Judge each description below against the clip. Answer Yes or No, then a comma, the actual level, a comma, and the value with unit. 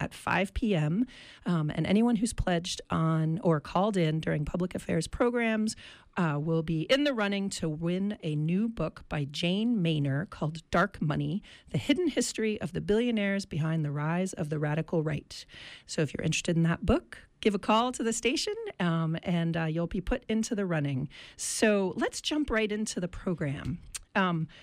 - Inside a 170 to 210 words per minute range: Yes, average, 185 wpm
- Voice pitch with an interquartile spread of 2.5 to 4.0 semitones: No, wide, 5.4 semitones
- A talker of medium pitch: Yes, medium, 180 Hz